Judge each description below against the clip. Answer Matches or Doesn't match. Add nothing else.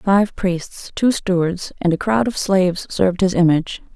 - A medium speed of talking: Matches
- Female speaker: Matches